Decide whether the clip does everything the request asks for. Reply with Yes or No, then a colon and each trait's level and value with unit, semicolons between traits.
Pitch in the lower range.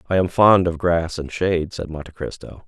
Yes: very low, 85 Hz